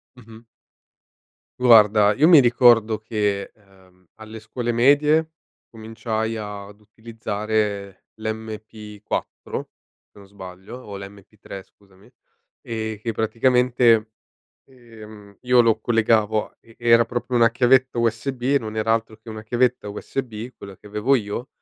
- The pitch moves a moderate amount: No, narrow, 2.2 semitones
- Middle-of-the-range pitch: No, low, 110 Hz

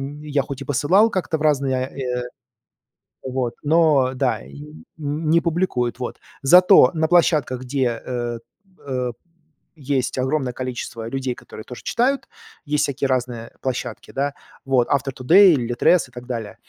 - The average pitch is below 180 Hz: Yes, low, 135 Hz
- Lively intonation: No, average, 3.5 semitones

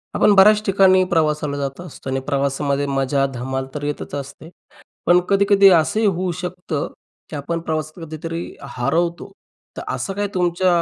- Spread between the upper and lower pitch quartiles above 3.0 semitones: Yes, average, 4.7 semitones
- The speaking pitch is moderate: Yes, medium, 160 Hz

